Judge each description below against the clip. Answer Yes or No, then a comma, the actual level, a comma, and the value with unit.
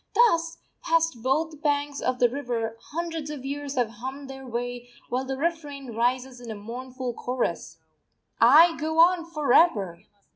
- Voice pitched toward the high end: Yes, very high, 270 Hz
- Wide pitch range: No, average, 4.3 semitones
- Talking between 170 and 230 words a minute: No, average, 155 wpm